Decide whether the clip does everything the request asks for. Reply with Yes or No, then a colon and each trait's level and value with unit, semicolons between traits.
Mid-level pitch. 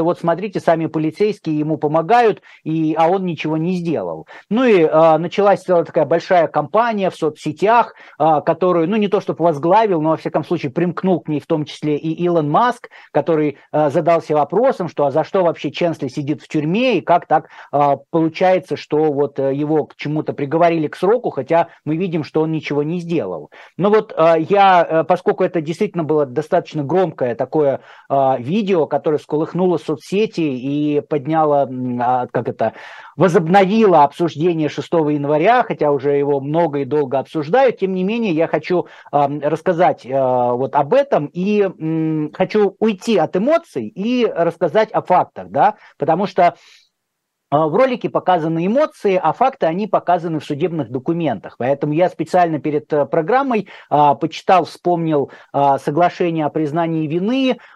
Yes: medium, 165 Hz